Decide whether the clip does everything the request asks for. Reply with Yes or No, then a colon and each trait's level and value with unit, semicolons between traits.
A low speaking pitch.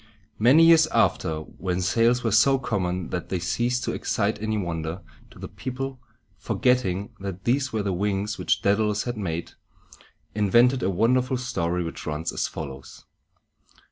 Yes: low, 105 Hz